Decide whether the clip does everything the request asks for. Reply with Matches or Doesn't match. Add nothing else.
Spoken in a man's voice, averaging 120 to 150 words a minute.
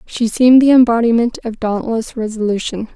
Doesn't match